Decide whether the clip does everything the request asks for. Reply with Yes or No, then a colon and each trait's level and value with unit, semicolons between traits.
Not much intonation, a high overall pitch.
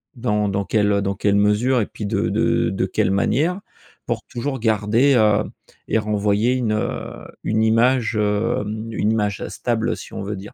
No: narrow, 2.3 semitones; low, 105 Hz